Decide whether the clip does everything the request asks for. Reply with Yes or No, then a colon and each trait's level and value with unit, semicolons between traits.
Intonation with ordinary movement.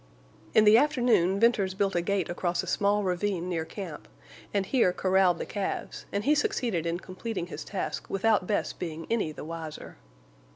Yes: average, 3.2 semitones